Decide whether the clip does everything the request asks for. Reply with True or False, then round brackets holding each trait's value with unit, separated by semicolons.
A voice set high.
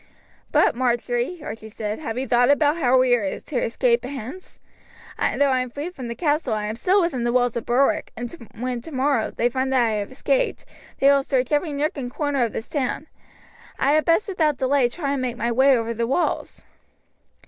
True (255 Hz)